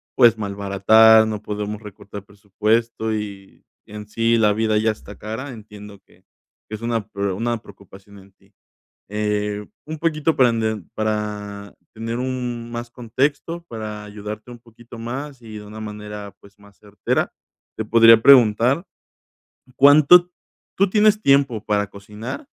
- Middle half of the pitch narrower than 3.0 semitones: Yes, narrow, 2.4 semitones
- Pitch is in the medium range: No, low, 110 Hz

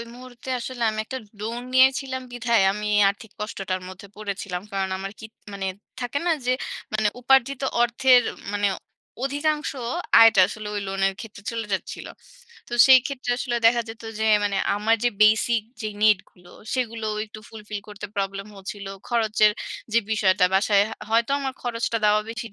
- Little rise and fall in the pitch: No, average, 3.1 semitones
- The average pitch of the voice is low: No, high, 220 Hz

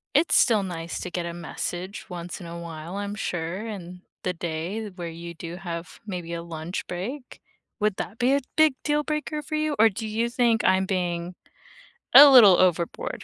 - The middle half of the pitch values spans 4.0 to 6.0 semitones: Yes, average, 4.8 semitones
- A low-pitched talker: No, medium, 185 Hz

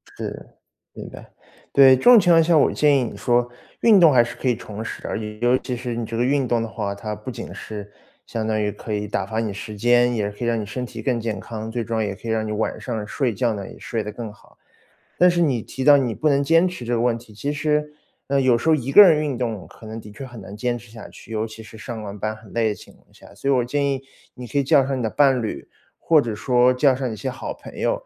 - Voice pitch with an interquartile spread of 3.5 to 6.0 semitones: Yes, average, 3.8 semitones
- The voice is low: Yes, low, 120 Hz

